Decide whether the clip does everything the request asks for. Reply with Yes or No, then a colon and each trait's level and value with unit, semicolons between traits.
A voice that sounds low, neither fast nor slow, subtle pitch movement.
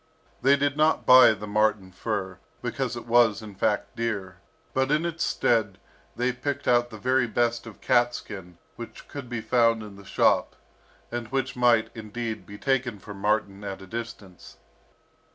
No: low, 115 Hz; average, 170 wpm; average, 3.2 semitones